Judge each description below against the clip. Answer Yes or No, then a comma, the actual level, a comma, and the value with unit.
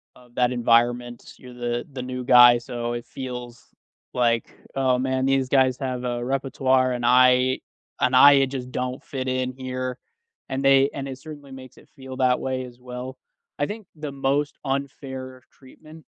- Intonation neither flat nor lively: No, narrow, 1.4 semitones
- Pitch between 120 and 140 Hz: Yes, low, 130 Hz